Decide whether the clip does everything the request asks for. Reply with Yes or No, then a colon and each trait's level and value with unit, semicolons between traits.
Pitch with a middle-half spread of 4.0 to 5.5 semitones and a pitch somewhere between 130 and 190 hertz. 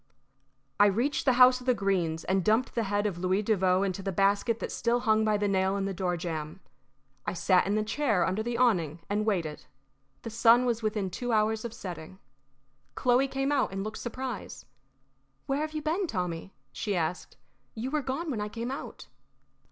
No: average, 4.5 semitones; high, 215 Hz